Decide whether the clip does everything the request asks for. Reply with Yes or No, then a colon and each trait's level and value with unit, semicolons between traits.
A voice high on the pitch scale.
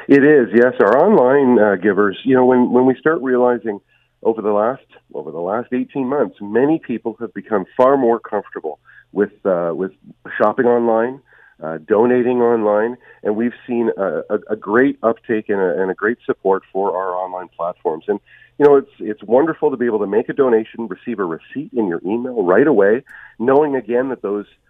No: low, 120 Hz